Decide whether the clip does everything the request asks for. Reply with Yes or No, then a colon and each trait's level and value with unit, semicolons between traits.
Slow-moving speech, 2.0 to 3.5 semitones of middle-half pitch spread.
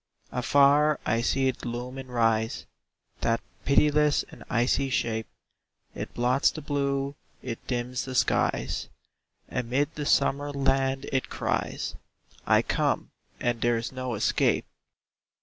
Yes: slow, 130 wpm; narrow, 2.6 semitones